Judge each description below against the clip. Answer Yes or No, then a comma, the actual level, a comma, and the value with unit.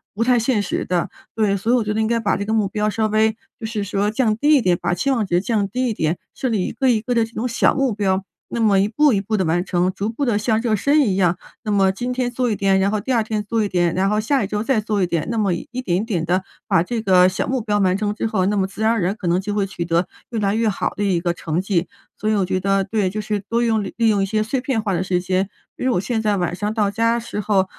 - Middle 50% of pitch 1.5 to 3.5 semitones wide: Yes, average, 3.1 semitones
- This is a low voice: No, high, 210 Hz